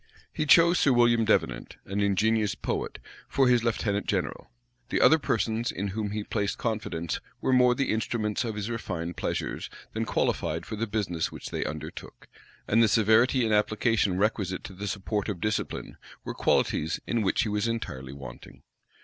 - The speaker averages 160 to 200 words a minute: Yes, average, 175 wpm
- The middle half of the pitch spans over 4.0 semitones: No, average, 2.8 semitones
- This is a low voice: Yes, low, 105 Hz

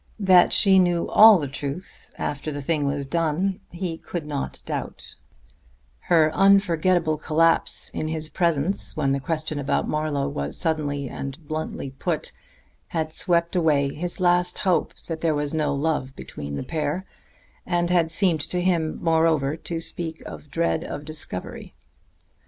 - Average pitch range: Yes, average, 3.1 semitones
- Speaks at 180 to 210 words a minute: No, average, 150 wpm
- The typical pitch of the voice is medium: Yes, medium, 160 Hz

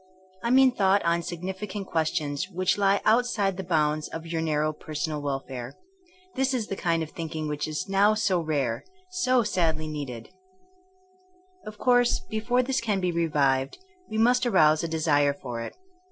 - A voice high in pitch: No, medium, 170 Hz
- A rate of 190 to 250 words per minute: No, average, 170 wpm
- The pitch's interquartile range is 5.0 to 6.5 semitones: Yes, wide, 5.6 semitones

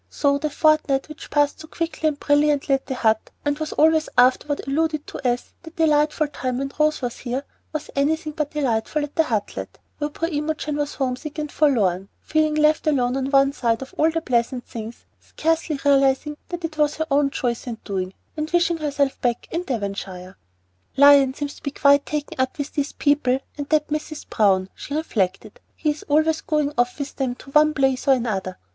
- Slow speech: No, average, 195 wpm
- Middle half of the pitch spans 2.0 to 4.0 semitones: Yes, average, 3.3 semitones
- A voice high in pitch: Yes, very high, 285 Hz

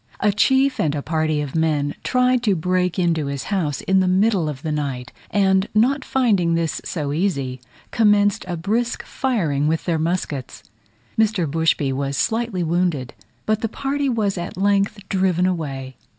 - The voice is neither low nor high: Yes, medium, 180 Hz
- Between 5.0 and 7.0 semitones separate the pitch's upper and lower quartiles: Yes, wide, 5.4 semitones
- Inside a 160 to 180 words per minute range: Yes, average, 165 wpm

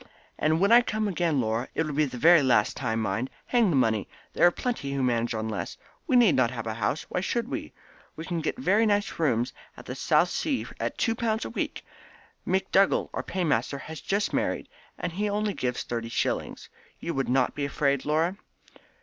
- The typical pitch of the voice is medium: Yes, medium, 155 Hz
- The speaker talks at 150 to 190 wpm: No, average, 200 wpm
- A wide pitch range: Yes, wide, 8.1 semitones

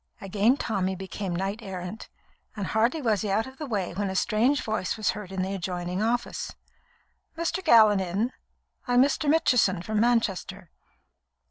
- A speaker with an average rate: Yes, average, 160 wpm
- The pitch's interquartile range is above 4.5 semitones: No, average, 3.9 semitones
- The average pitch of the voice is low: No, high, 210 Hz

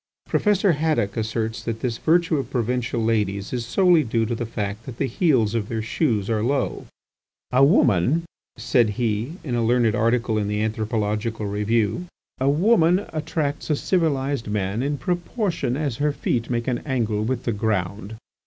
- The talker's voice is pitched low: Yes, low, 120 Hz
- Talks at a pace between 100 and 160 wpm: No, average, 170 wpm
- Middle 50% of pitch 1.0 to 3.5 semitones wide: No, average, 4.7 semitones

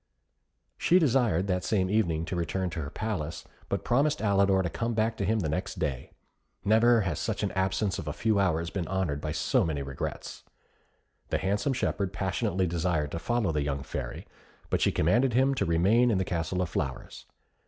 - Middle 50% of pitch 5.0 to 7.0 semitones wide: Yes, wide, 5.4 semitones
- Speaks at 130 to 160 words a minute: No, average, 190 wpm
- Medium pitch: No, very low, 95 Hz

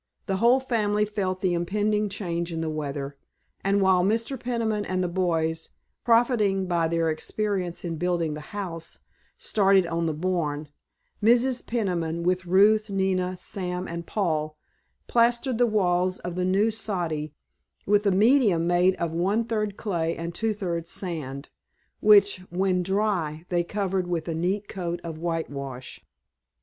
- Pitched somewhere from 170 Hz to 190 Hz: Yes, medium, 185 Hz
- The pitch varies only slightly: No, average, 3.7 semitones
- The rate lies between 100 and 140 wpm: No, average, 150 wpm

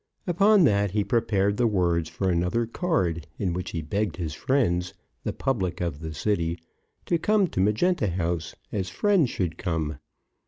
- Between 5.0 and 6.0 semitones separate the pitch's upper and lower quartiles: Yes, wide, 5.6 semitones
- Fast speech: No, average, 165 wpm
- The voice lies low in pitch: Yes, very low, 95 Hz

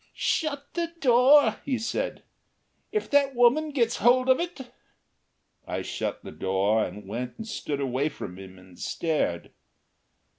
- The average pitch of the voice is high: Yes, high, 235 Hz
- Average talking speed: Yes, average, 150 wpm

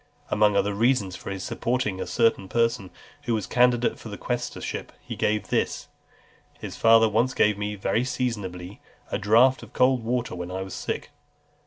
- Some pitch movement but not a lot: Yes, average, 3.5 semitones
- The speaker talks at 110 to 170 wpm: No, average, 185 wpm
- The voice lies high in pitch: No, low, 110 Hz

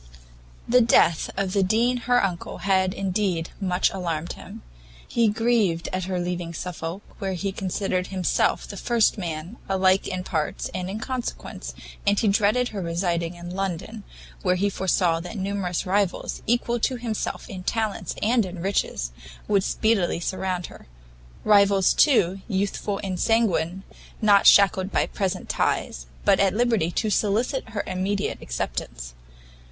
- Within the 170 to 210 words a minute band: No, average, 150 wpm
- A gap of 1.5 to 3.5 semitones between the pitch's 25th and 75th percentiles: Yes, average, 2.9 semitones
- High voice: Yes, high, 195 Hz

